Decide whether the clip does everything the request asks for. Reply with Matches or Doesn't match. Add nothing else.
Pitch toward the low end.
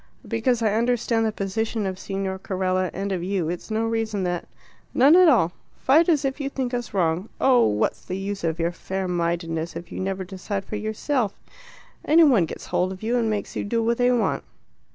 Doesn't match